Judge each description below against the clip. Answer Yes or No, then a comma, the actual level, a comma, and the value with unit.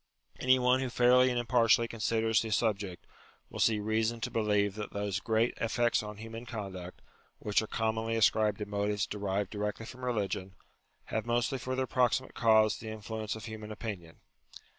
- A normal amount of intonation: No, narrow, 2.2 semitones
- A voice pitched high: No, low, 110 Hz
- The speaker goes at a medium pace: Yes, average, 170 wpm